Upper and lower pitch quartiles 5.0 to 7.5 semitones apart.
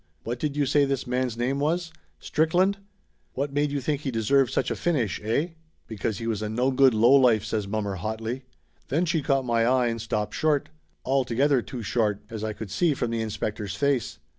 No: average, 4.2 semitones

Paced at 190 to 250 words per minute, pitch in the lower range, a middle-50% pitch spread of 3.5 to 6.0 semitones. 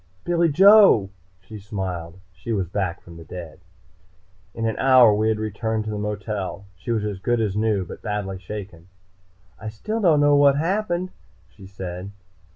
No: average, 170 wpm; low, 105 Hz; average, 4.8 semitones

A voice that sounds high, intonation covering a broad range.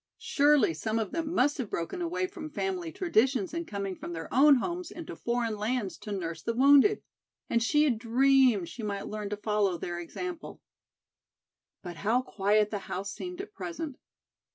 Yes: high, 240 Hz; wide, 7.6 semitones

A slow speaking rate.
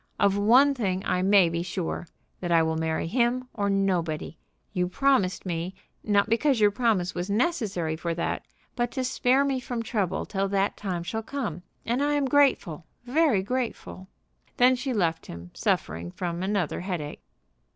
No: average, 170 wpm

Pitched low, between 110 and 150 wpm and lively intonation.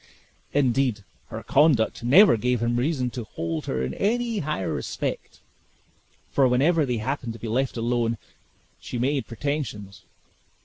No: low, 125 Hz; average, 140 wpm; average, 4.0 semitones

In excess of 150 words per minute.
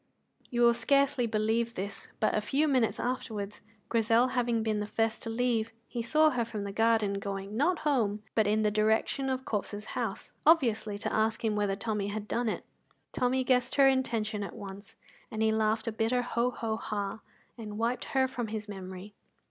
Yes: average, 190 wpm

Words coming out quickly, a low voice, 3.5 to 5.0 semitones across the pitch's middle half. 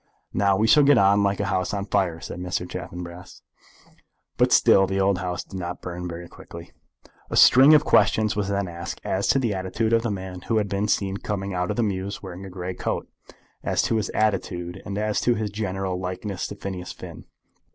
No: fast, 215 wpm; very low, 95 Hz; narrow, 2.4 semitones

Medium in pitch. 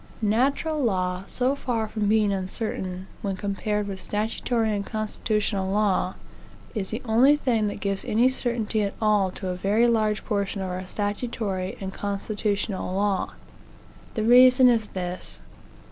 No: high, 210 Hz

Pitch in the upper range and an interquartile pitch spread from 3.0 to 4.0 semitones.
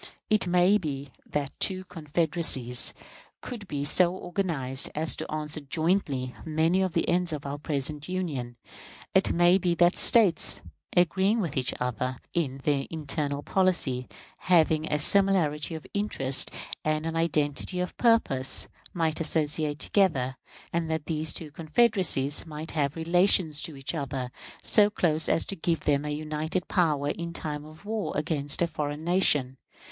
No: medium, 155 Hz; average, 3.5 semitones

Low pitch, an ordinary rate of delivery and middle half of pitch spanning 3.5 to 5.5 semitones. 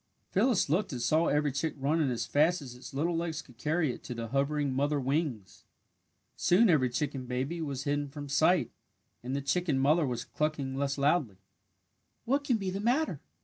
No: medium, 145 Hz; average, 190 wpm; average, 3.8 semitones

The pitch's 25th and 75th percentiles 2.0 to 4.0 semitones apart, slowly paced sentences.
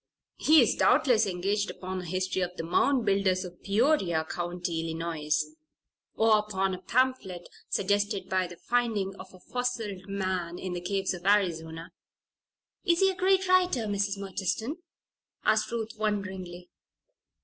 No: average, 3.6 semitones; average, 145 wpm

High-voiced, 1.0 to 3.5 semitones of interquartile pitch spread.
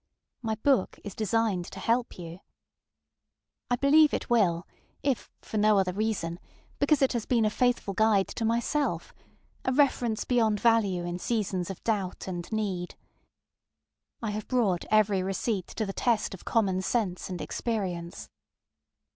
No: high, 215 Hz; average, 3.9 semitones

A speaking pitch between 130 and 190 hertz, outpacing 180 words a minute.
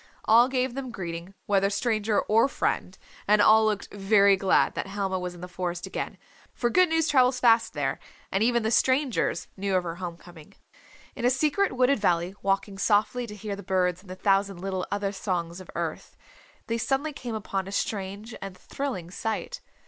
No: high, 200 Hz; average, 190 wpm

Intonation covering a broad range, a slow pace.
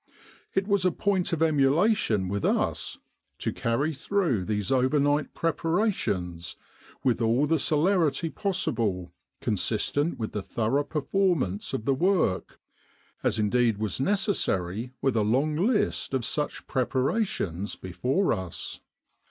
Yes: wide, 7.8 semitones; slow, 125 wpm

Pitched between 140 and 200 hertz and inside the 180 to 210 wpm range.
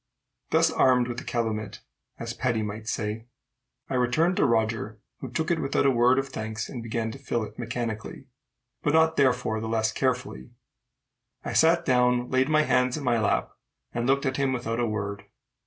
No: low, 120 Hz; average, 190 wpm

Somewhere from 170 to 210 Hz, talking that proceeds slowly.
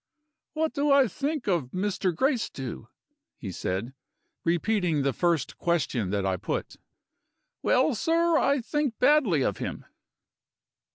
Yes: medium, 185 Hz; slow, 125 wpm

